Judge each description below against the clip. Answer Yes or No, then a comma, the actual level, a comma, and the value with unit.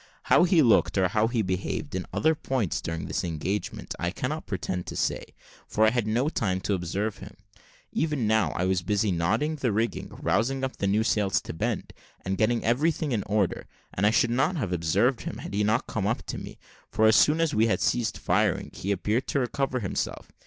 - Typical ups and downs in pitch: Yes, average, 4.7 semitones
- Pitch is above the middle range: No, low, 110 Hz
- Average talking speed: No, fast, 210 wpm